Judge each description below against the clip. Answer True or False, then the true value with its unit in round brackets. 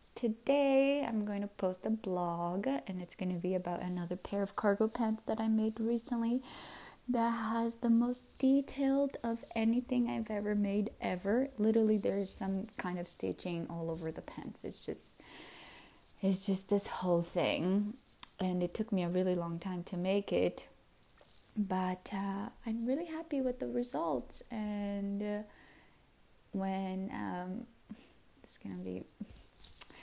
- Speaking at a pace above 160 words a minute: False (155 wpm)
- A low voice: False (205 Hz)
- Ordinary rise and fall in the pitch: True (4.0 semitones)